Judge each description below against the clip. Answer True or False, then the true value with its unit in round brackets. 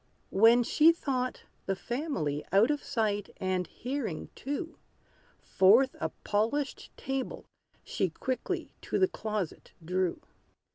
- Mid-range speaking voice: False (230 Hz)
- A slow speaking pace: True (115 wpm)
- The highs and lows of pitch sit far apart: True (6.2 semitones)